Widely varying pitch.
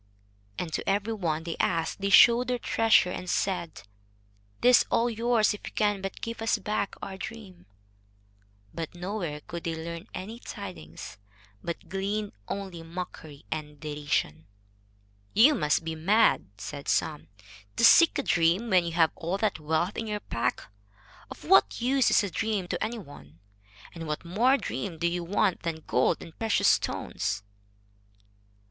No: average, 4.8 semitones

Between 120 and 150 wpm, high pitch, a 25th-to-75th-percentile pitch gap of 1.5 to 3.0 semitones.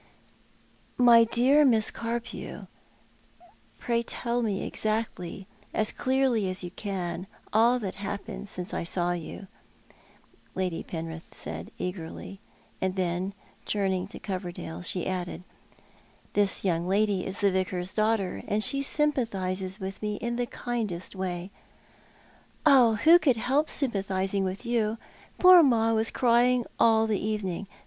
No: slow, 135 wpm; high, 205 Hz; average, 4.0 semitones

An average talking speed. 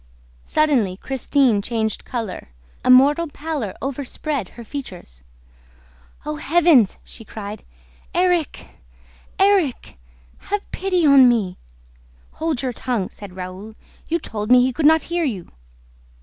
No: slow, 120 wpm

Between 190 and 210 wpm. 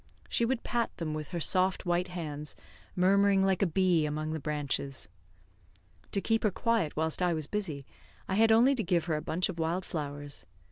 Yes: average, 195 wpm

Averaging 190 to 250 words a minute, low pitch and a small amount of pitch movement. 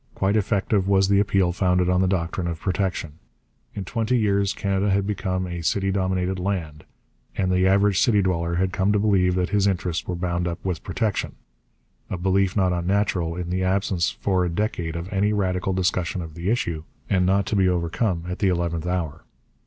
Yes: average, 195 wpm; very low, 95 Hz; narrow, 2.0 semitones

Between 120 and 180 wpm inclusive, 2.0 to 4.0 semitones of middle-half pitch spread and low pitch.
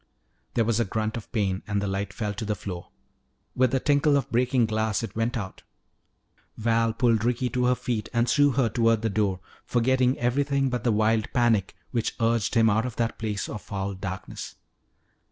No: average, 195 wpm; average, 2.7 semitones; low, 115 Hz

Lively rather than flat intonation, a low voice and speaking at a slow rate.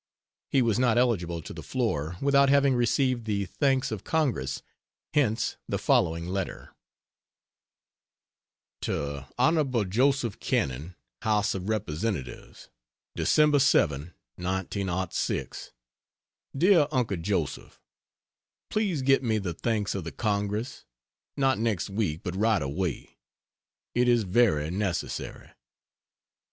Yes: wide, 6.4 semitones; low, 105 Hz; slow, 110 wpm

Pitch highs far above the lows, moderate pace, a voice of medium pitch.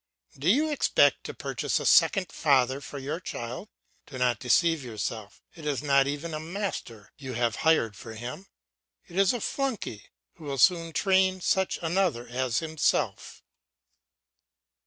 Yes: wide, 6.8 semitones; average, 155 wpm; medium, 150 Hz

